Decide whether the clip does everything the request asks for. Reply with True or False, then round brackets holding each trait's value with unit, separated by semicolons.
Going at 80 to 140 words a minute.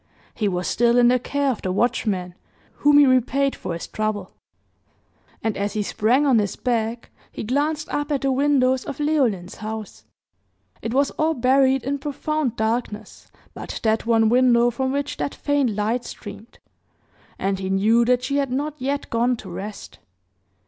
False (170 wpm)